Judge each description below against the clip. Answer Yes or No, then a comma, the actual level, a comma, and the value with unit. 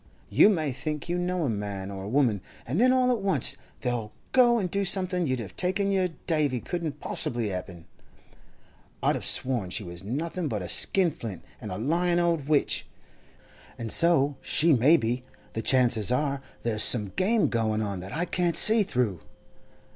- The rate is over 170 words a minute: Yes, average, 180 wpm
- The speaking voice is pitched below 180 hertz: Yes, medium, 140 Hz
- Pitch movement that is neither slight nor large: No, wide, 8.1 semitones